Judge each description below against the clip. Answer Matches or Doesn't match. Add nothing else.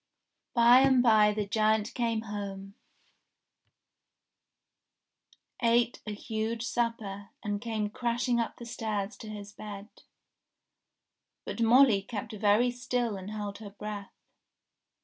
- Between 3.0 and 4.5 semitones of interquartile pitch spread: Doesn't match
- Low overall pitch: Doesn't match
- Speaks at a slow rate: Matches